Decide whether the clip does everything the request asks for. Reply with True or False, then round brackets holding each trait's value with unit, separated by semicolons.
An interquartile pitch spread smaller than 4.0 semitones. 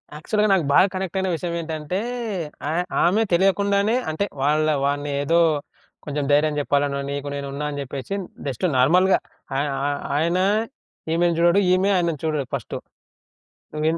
False (4.3 semitones)